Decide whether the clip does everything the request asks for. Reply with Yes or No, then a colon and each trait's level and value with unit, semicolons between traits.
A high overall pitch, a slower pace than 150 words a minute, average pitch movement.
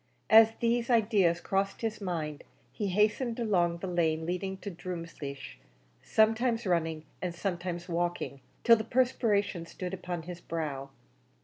No: medium, 180 Hz; slow, 135 wpm; average, 4.4 semitones